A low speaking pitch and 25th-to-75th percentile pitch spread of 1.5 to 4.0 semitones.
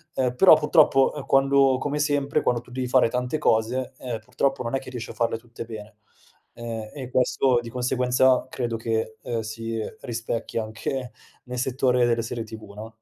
Yes: low, 125 Hz; narrow, 2.4 semitones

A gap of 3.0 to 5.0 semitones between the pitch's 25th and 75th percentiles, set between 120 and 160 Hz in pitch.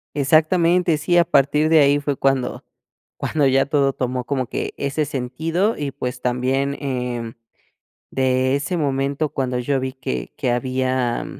No: narrow, 2.6 semitones; low, 135 Hz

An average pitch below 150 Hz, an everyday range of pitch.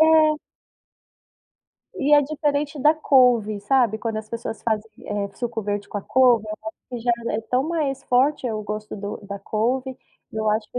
No: high, 235 Hz; average, 4.1 semitones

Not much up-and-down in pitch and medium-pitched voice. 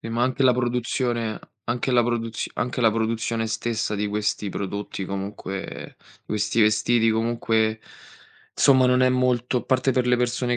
No: narrow, 2.2 semitones; low, 115 Hz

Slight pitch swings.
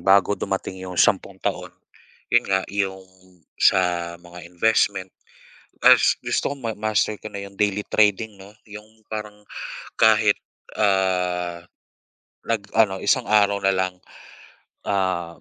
Yes: narrow, 2.3 semitones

